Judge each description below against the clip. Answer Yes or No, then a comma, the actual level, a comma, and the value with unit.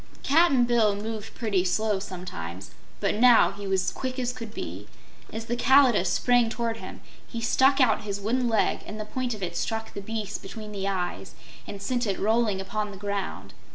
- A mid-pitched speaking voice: No, high, 215 Hz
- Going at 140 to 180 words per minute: No, average, 190 wpm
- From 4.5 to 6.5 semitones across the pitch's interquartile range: No, average, 3.3 semitones